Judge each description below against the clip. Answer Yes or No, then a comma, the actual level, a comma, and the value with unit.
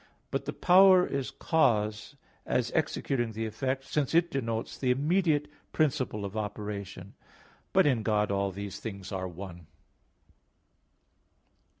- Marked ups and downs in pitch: Yes, wide, 6.0 semitones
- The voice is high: No, low, 115 Hz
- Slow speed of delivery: Yes, slow, 125 wpm